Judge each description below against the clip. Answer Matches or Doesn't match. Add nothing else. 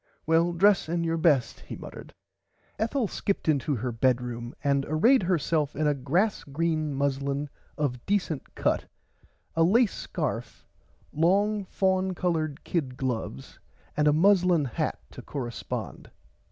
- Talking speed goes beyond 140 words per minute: Doesn't match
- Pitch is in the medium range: Matches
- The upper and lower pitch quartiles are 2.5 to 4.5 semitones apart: Doesn't match